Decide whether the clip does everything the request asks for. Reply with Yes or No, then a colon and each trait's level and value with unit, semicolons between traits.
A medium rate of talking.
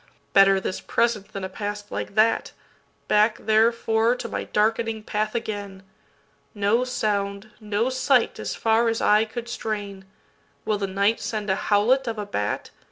Yes: average, 145 wpm